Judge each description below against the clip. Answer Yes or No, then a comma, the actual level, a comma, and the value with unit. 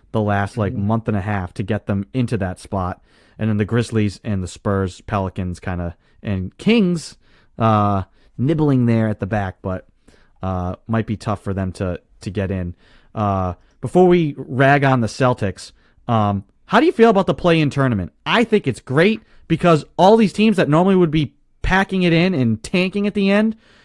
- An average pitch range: No, wide, 8.7 semitones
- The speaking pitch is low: Yes, low, 115 Hz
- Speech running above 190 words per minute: Yes, average, 200 wpm